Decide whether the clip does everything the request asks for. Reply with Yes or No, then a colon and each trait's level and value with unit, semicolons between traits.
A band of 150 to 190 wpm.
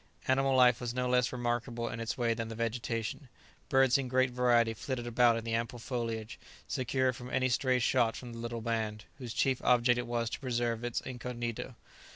No: average, 200 wpm